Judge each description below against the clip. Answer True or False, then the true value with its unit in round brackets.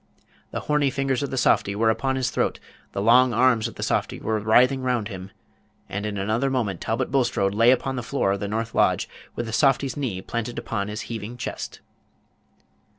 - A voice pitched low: True (115 Hz)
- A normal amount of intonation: True (3.4 semitones)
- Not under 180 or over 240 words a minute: True (200 wpm)